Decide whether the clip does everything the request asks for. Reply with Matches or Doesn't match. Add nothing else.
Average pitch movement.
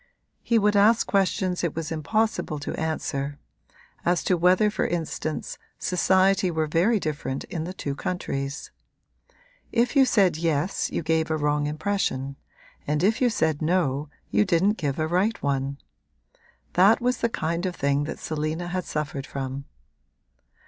Matches